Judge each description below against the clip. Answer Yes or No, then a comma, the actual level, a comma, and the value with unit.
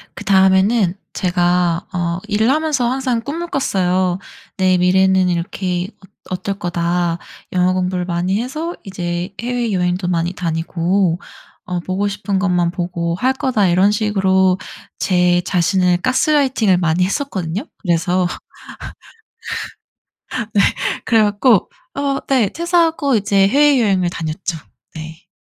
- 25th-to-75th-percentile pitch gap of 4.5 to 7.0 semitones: No, average, 3.7 semitones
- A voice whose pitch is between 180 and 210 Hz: Yes, high, 190 Hz